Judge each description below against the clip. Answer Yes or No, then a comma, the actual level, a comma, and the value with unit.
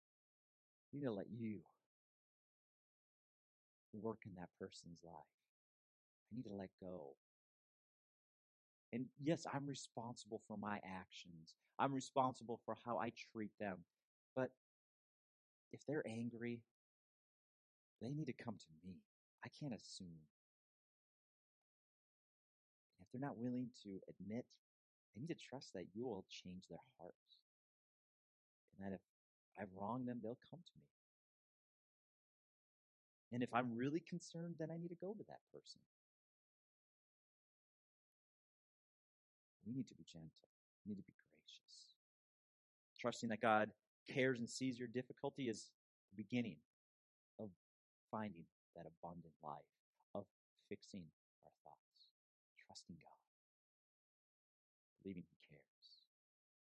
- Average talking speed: No, slow, 120 wpm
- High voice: No, low, 110 Hz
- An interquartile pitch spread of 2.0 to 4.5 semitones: No, wide, 5.6 semitones